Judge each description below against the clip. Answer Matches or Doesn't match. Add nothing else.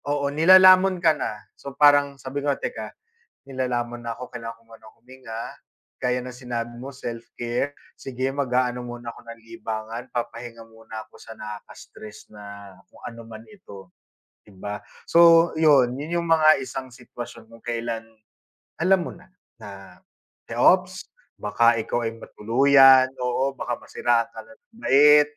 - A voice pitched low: Matches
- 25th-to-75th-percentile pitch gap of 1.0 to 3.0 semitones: Doesn't match